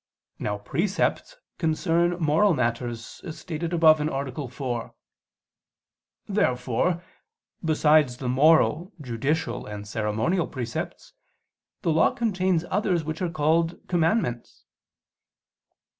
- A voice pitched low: No, medium, 155 Hz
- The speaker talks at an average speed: No, slow, 100 wpm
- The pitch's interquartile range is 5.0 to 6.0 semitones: Yes, wide, 5.5 semitones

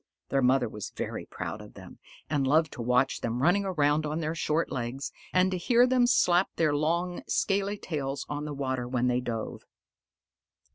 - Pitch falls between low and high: Yes, medium, 150 Hz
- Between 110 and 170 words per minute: No, average, 185 wpm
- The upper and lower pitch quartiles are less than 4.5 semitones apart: No, average, 5.3 semitones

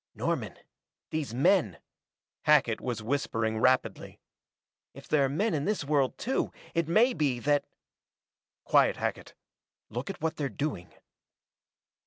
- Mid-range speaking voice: Yes, medium, 145 Hz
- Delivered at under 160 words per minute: Yes, average, 140 wpm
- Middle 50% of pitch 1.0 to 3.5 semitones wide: No, average, 4.6 semitones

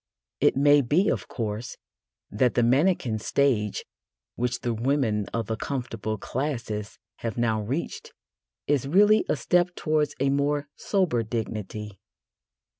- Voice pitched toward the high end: No, low, 125 Hz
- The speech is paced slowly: Yes, slow, 130 wpm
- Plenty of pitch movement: No, average, 4.8 semitones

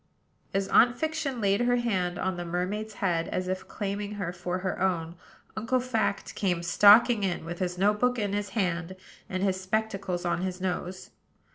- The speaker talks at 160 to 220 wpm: Yes, average, 180 wpm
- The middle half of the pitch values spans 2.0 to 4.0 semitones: Yes, average, 3.2 semitones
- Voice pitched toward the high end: Yes, high, 195 Hz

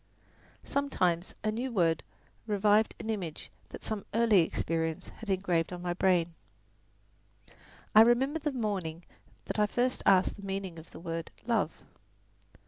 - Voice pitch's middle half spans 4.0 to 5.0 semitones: Yes, average, 4.6 semitones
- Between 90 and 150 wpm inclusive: Yes, average, 140 wpm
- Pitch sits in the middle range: No, high, 195 Hz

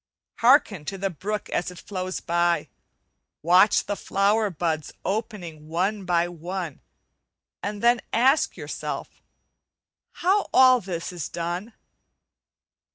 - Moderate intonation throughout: Yes, average, 3.7 semitones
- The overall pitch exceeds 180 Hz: Yes, high, 190 Hz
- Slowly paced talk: Yes, slow, 115 wpm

